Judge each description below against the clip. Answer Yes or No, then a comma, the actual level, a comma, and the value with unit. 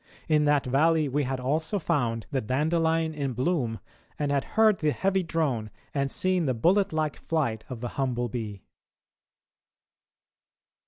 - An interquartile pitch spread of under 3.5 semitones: No, average, 4.4 semitones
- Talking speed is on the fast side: No, average, 150 wpm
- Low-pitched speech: No, medium, 145 Hz